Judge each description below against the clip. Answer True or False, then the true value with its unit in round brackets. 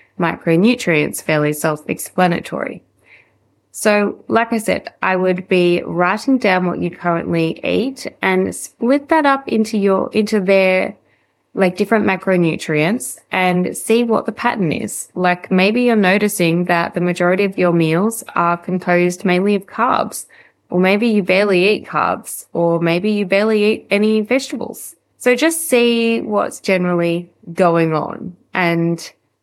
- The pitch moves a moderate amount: True (4.0 semitones)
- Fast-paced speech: False (145 wpm)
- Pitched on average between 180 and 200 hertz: True (185 Hz)